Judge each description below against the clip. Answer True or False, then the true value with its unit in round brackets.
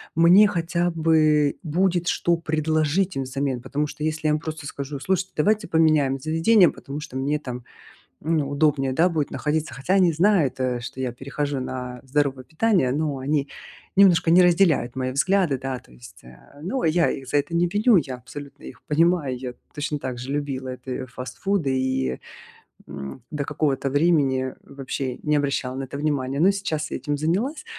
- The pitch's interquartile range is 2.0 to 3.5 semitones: False (3.9 semitones)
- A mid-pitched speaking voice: True (150 Hz)